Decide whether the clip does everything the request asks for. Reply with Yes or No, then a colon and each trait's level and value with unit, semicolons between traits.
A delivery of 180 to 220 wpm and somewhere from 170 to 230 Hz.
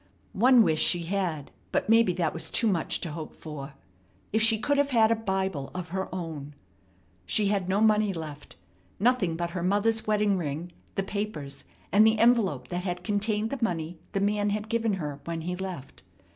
Yes: average, 190 wpm; high, 190 Hz